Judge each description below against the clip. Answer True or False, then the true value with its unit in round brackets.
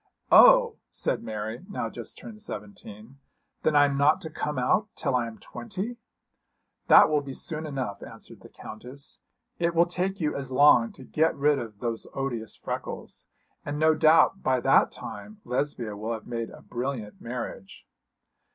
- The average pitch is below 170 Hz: True (140 Hz)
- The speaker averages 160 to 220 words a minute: True (170 wpm)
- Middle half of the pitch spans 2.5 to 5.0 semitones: False (5.4 semitones)